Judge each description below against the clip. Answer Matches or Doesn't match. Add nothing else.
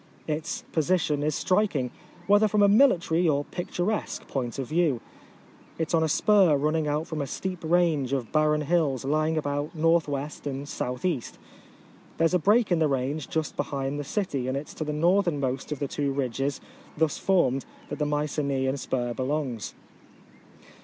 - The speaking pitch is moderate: Matches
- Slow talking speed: Doesn't match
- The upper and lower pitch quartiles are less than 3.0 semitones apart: Doesn't match